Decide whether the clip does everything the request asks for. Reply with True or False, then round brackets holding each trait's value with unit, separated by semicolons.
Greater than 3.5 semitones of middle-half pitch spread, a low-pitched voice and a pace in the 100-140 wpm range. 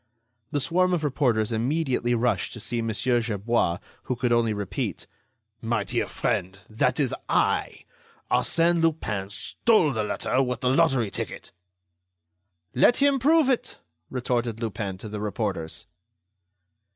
True (5.4 semitones; 120 Hz; 135 wpm)